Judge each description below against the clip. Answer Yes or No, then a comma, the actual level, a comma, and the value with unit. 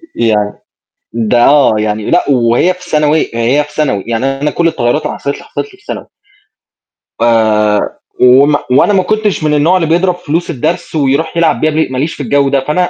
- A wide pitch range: Yes, wide, 5.8 semitones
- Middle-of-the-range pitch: Yes, medium, 145 Hz